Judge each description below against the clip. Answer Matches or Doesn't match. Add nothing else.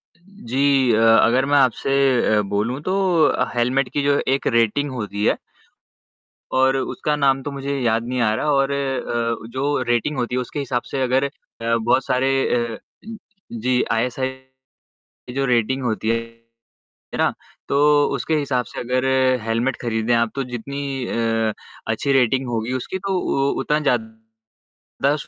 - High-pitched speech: Doesn't match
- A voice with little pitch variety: Doesn't match